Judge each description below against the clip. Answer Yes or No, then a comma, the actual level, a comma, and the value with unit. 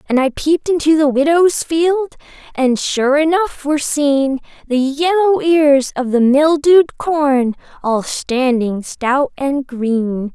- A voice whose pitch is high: Yes, very high, 285 Hz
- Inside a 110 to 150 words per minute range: Yes, average, 140 wpm